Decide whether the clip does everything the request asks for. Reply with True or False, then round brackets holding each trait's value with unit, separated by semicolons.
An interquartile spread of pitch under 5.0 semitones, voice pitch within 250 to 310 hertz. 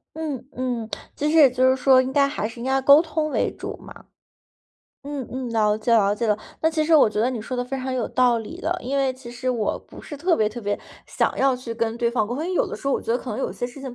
True (3.0 semitones; 255 Hz)